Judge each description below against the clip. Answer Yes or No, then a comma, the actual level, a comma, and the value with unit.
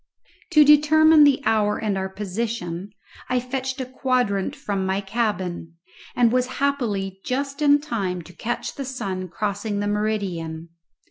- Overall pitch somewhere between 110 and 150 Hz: No, high, 215 Hz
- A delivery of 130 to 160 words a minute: Yes, average, 145 wpm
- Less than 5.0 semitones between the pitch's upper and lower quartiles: No, average, 5.3 semitones